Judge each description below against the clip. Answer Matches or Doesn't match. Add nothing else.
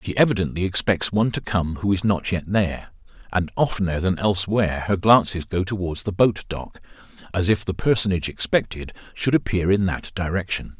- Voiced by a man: Matches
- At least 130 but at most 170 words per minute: Doesn't match